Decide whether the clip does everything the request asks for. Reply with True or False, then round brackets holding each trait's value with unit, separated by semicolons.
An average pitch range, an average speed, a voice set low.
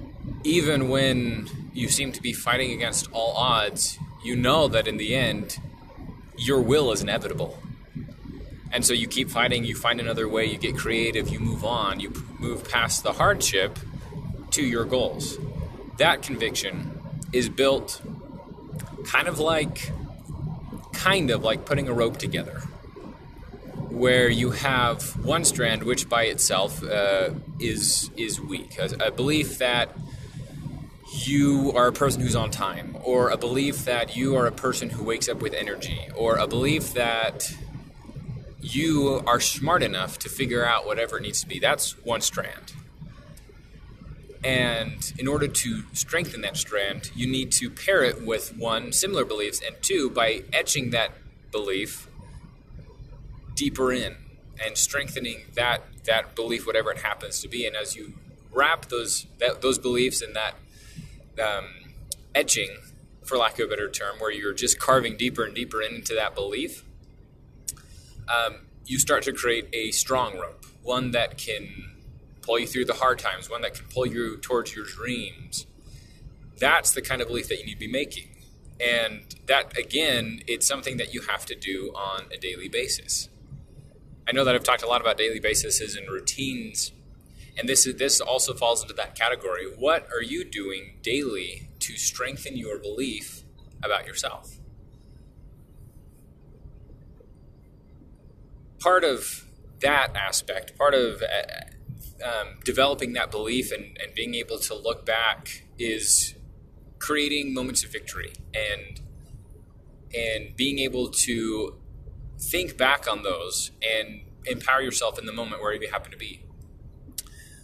True (3.0 semitones; 155 wpm; 125 Hz)